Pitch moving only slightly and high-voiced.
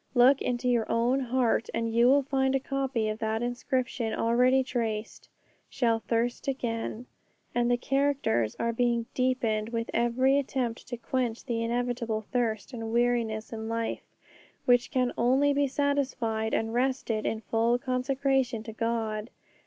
Yes: narrow, 2.3 semitones; high, 240 Hz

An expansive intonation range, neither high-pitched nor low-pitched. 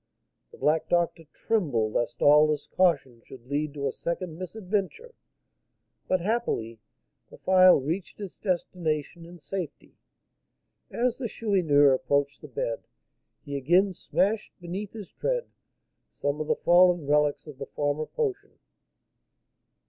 No: average, 5.0 semitones; medium, 170 Hz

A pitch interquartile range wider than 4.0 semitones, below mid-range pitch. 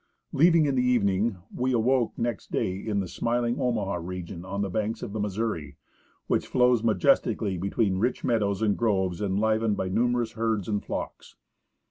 No: average, 3.4 semitones; low, 110 Hz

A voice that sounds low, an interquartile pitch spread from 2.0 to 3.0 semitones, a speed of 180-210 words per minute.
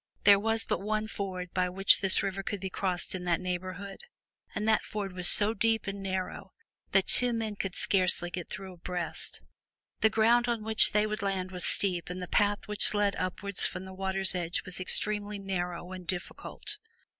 No: high, 195 Hz; narrow, 2.4 semitones; average, 190 wpm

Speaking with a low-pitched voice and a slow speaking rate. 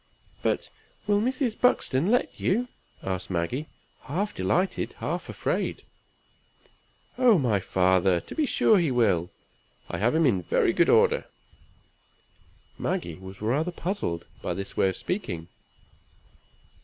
Yes: low, 130 Hz; slow, 130 wpm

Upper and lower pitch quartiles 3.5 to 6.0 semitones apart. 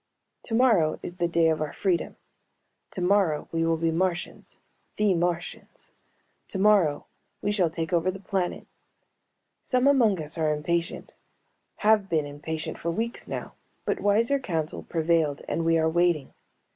Yes: average, 3.9 semitones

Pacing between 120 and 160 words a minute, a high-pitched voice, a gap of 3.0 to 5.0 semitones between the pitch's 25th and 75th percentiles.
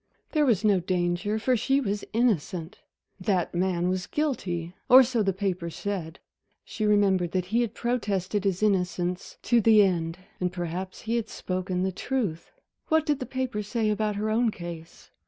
No: average, 175 wpm; high, 200 Hz; average, 4.0 semitones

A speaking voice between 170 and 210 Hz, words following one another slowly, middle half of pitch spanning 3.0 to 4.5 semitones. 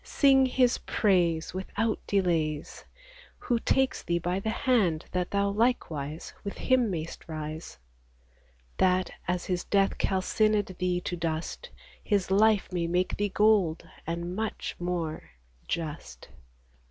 Yes: medium, 185 Hz; slow, 130 wpm; average, 3.9 semitones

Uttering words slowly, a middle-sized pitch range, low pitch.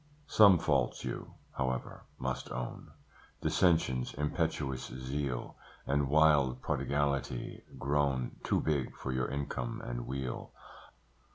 No: slow, 105 wpm; narrow, 2.2 semitones; very low, 70 Hz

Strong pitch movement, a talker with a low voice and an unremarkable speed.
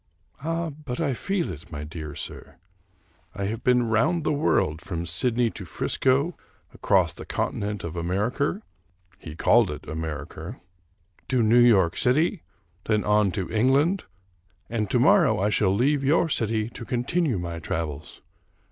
Yes: wide, 7.9 semitones; low, 110 Hz; average, 155 wpm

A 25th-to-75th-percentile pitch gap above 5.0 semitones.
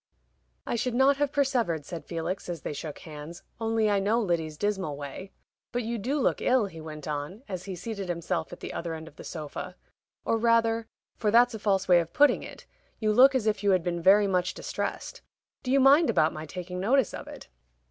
Yes: wide, 5.6 semitones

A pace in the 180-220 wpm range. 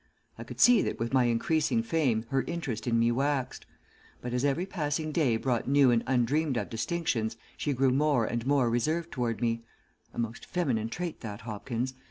Yes: average, 190 wpm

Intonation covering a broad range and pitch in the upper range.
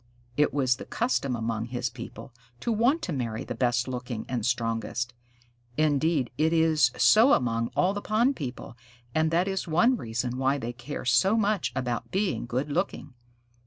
No: wide, 6.9 semitones; low, 135 Hz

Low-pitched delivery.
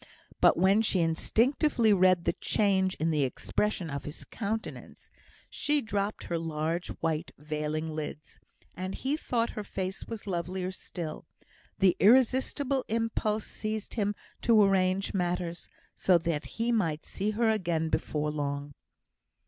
No: medium, 185 Hz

